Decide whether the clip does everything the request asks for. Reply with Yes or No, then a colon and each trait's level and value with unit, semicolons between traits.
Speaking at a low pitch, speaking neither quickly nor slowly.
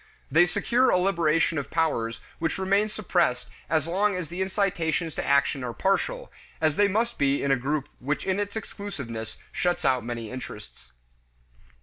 No: medium, 165 Hz; average, 165 wpm